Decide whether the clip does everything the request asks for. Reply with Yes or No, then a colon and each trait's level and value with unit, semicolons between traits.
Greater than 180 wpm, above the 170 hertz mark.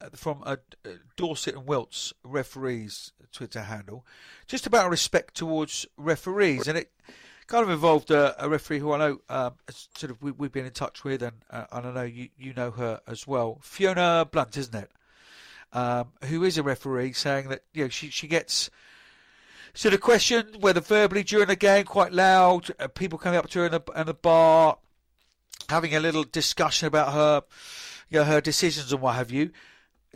No: average, 195 wpm; medium, 150 Hz